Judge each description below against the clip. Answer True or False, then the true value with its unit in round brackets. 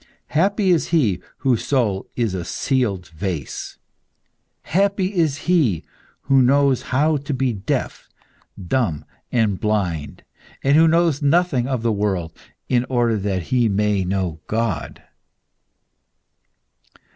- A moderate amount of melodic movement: False (6.6 semitones)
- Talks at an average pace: False (120 wpm)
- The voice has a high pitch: False (120 Hz)